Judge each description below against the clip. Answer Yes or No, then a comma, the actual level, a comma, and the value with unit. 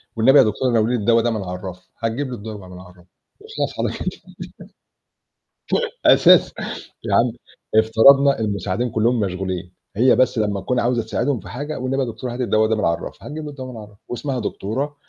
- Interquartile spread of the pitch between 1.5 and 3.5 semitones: No, average, 4.0 semitones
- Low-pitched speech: Yes, low, 115 Hz